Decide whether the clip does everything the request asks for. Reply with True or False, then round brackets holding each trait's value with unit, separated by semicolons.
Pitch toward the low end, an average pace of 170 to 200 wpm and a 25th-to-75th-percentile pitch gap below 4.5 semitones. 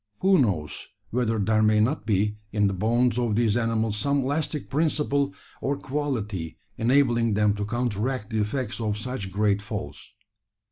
False (110 Hz; 155 wpm; 3.8 semitones)